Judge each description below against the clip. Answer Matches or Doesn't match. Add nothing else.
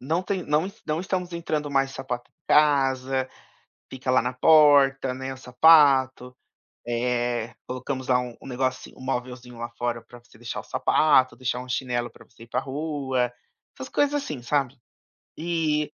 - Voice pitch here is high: Doesn't match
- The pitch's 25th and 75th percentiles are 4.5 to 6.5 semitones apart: Doesn't match